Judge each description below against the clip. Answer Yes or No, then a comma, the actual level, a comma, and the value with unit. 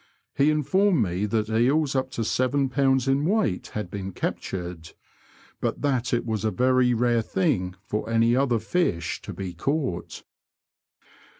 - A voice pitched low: Yes, low, 120 Hz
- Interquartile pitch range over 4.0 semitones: Yes, average, 5.2 semitones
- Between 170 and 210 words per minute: No, average, 155 wpm